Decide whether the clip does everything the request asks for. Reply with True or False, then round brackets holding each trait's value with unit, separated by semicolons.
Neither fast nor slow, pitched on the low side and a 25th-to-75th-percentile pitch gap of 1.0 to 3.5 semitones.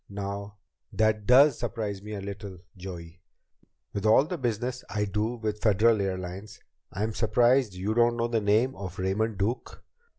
True (160 wpm; 105 Hz; 2.9 semitones)